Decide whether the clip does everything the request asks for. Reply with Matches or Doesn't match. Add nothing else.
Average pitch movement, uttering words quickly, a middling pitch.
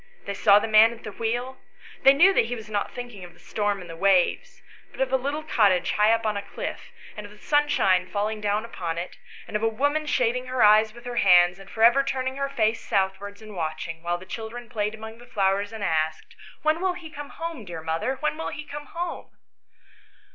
Doesn't match